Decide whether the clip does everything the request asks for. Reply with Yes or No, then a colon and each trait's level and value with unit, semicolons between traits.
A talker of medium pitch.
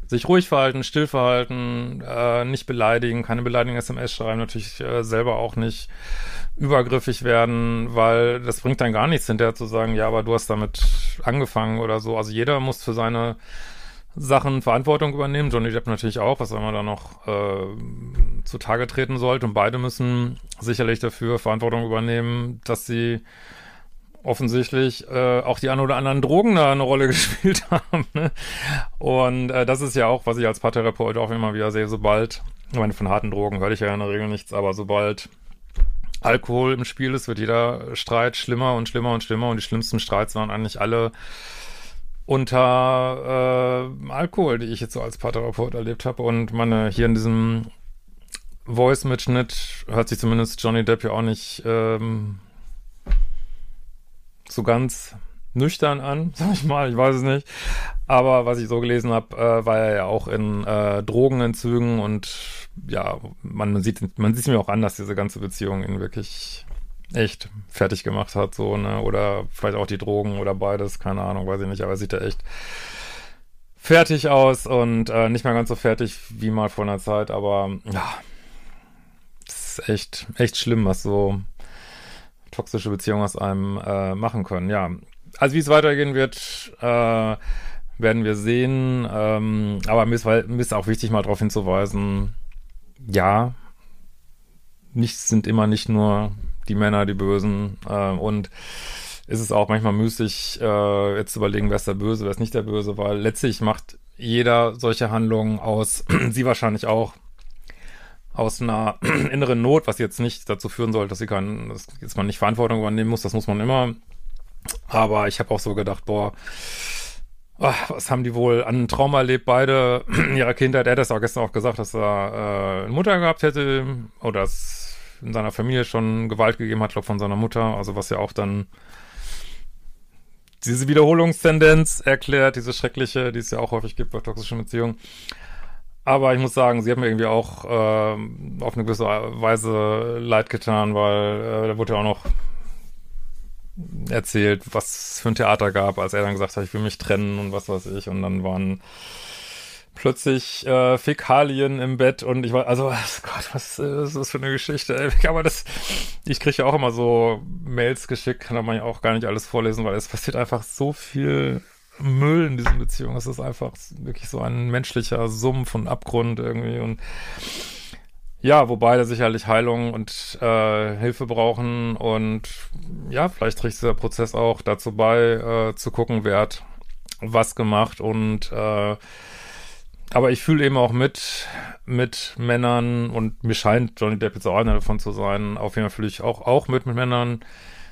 No: low, 115 Hz